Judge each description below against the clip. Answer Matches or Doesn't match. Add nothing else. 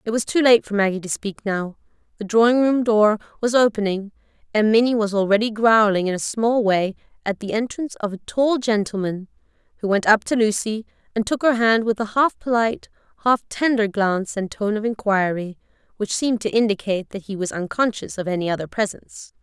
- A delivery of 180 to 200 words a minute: Matches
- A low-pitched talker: Doesn't match